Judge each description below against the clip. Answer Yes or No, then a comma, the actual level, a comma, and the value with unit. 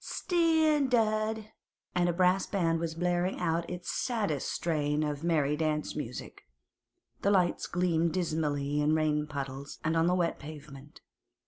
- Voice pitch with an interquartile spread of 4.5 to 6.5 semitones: No, average, 3.4 semitones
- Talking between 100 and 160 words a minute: Yes, average, 140 wpm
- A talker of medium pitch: Yes, medium, 165 Hz